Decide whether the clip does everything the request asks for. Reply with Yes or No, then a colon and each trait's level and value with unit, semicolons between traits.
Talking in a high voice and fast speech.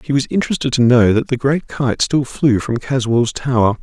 No: low, 130 Hz; fast, 220 wpm